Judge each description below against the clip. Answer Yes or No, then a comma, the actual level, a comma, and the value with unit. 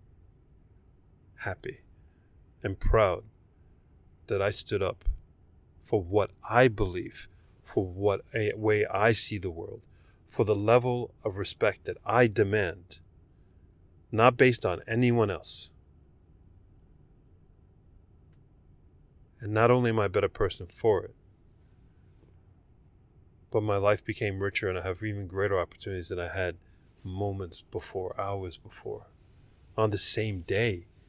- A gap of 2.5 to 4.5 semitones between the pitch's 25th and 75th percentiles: Yes, average, 3.5 semitones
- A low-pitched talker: Yes, very low, 95 Hz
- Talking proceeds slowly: Yes, slow, 125 wpm